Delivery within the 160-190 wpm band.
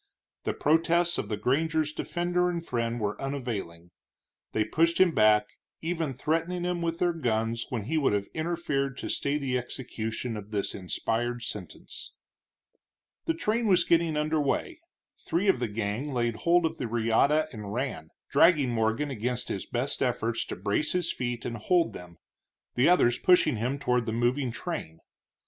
Yes: average, 165 wpm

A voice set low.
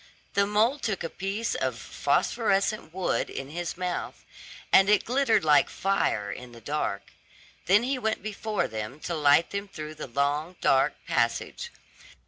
No: medium, 180 Hz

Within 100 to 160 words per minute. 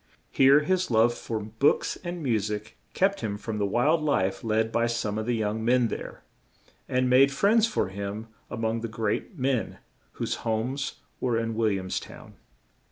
No: average, 180 wpm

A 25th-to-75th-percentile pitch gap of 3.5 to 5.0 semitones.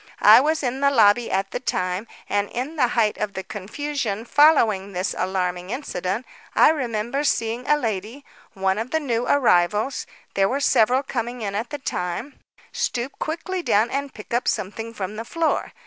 No: wide, 5.6 semitones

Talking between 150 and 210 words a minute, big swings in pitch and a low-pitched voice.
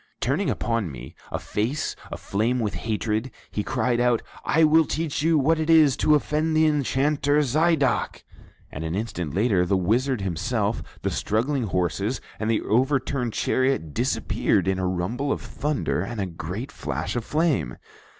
Yes: average, 160 wpm; wide, 6.4 semitones; low, 120 Hz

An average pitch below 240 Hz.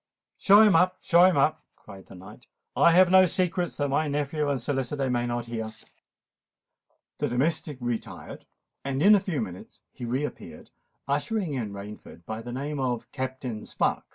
Yes: low, 135 Hz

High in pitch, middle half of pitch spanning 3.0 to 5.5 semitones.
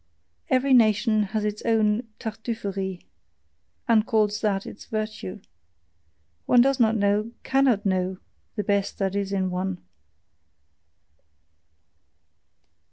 No: high, 210 Hz; narrow, 2.4 semitones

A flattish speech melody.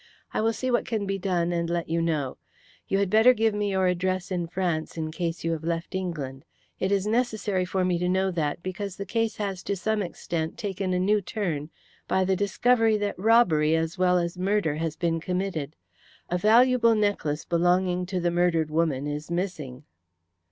No: average, 3.4 semitones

